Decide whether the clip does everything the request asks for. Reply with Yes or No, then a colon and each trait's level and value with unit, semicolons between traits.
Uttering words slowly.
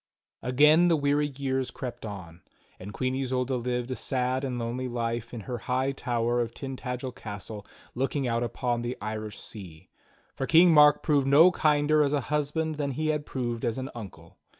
No: average, 180 wpm